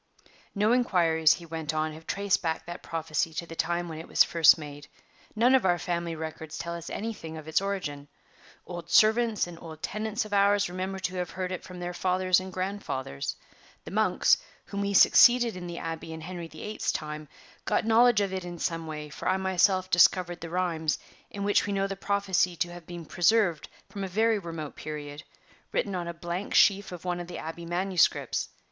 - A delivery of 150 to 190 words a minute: No, fast, 205 wpm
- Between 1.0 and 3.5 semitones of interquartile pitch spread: Yes, average, 3.2 semitones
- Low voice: No, medium, 175 Hz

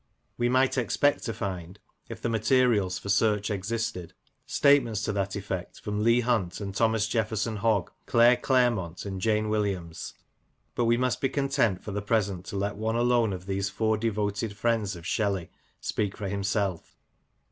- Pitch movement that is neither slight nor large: Yes, average, 3.0 semitones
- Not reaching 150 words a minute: No, average, 170 wpm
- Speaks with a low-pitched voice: Yes, low, 105 Hz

